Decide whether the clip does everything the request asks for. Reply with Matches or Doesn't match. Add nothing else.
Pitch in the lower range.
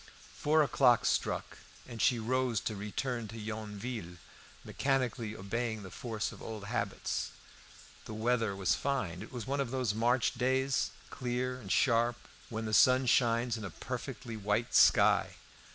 Matches